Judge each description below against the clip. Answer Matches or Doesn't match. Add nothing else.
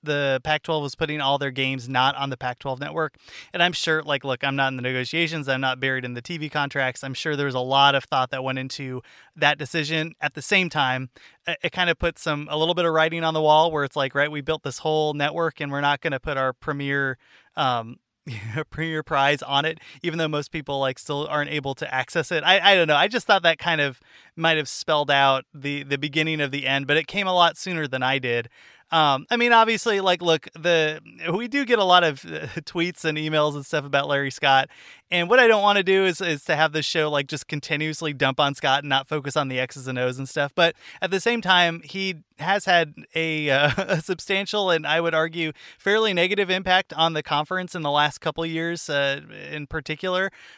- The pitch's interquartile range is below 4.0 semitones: Matches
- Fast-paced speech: Matches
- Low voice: Doesn't match